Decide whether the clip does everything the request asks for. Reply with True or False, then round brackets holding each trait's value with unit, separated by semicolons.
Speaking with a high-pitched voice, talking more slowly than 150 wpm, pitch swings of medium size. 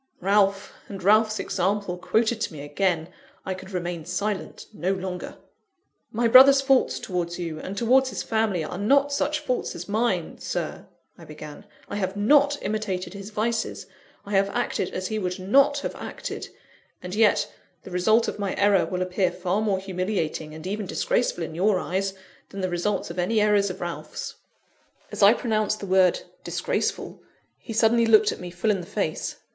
False (200 Hz; 175 wpm; 3.3 semitones)